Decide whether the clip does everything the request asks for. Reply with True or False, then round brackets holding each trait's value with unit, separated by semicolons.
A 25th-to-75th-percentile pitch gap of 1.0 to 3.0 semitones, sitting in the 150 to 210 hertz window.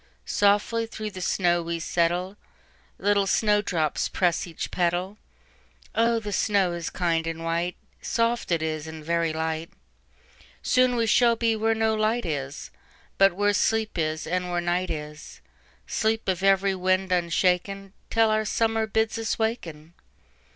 False (4.5 semitones; 185 Hz)